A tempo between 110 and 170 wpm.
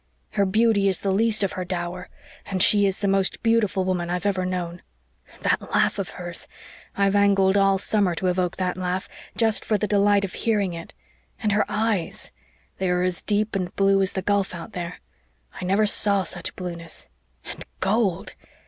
No: average, 185 wpm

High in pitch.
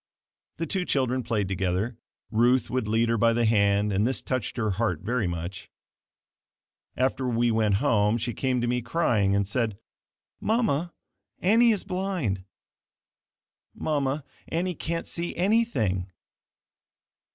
No: low, 120 Hz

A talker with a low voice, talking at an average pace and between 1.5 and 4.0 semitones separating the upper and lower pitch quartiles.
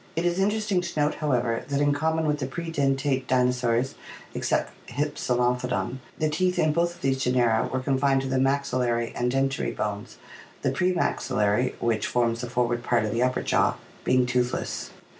Yes: low, 130 Hz; average, 175 wpm; average, 3.3 semitones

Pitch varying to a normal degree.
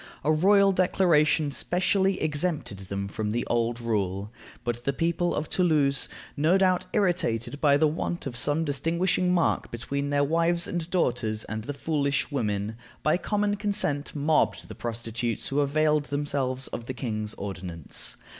No: wide, 6.3 semitones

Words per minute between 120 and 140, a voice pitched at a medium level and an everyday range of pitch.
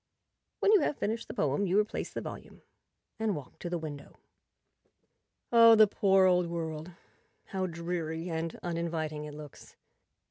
No: average, 150 wpm; medium, 170 Hz; average, 3.7 semitones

